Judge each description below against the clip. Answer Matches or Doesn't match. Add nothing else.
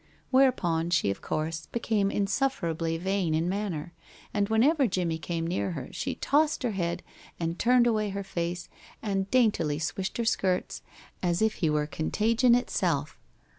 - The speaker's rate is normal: Matches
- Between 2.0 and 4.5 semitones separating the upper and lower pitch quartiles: Doesn't match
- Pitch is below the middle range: Doesn't match